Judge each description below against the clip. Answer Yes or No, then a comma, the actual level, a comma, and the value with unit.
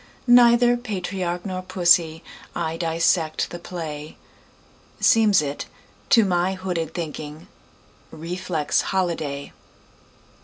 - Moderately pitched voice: Yes, medium, 175 Hz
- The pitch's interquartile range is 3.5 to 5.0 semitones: No, average, 2.8 semitones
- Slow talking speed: Yes, slow, 75 wpm